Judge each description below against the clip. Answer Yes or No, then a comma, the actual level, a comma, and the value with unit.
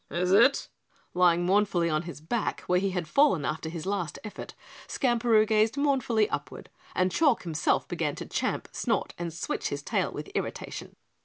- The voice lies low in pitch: No, medium, 185 Hz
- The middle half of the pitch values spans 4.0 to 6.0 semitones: Yes, average, 4.9 semitones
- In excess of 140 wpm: Yes, average, 170 wpm